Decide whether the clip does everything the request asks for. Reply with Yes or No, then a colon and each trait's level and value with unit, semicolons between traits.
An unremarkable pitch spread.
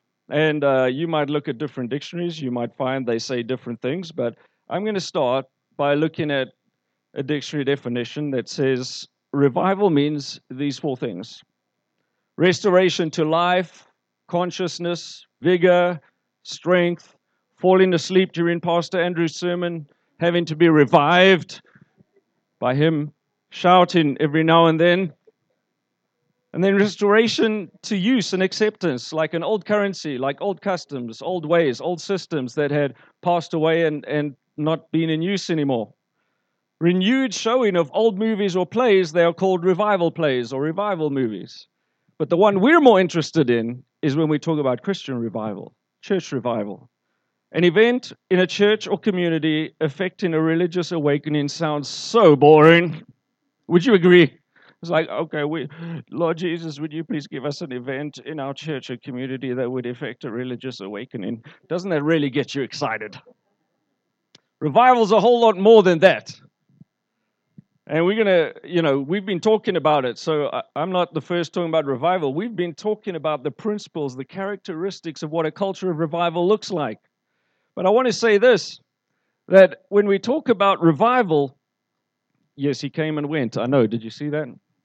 Yes: average, 4.5 semitones